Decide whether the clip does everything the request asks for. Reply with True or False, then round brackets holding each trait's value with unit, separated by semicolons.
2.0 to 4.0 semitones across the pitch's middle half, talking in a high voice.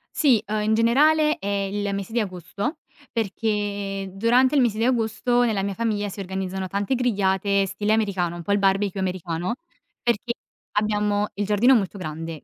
True (2.8 semitones; 205 Hz)